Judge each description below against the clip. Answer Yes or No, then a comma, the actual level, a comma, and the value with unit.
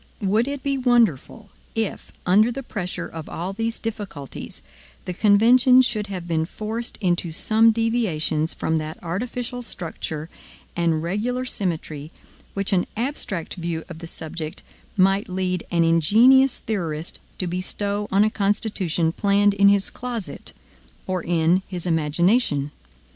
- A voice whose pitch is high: Yes, high, 195 Hz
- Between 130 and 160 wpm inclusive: Yes, slow, 135 wpm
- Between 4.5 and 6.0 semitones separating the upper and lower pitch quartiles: Yes, average, 5.2 semitones